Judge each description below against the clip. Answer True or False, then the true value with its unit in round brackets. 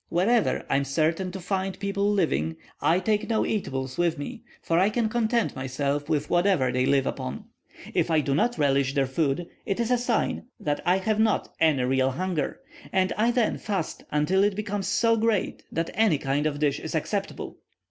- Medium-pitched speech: True (175 Hz)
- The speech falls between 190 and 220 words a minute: True (195 wpm)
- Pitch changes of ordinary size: False (6.9 semitones)